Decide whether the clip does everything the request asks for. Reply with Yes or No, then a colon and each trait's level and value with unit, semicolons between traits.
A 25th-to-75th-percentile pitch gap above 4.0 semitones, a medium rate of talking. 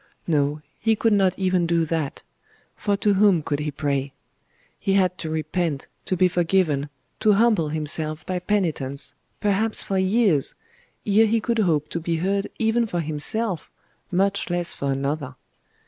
Yes: average, 4.8 semitones; average, 160 wpm